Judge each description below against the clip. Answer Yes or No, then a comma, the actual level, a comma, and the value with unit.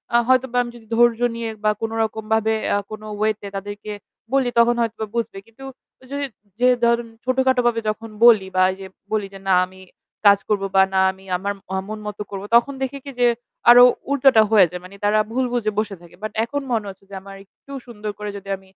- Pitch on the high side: Yes, high, 220 Hz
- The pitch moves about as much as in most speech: Yes, average, 3.1 semitones